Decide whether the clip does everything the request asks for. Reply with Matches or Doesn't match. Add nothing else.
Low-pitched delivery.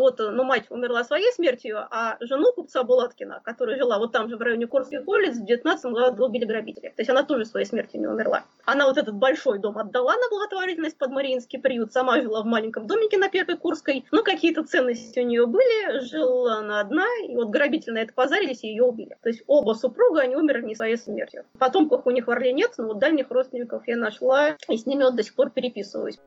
Doesn't match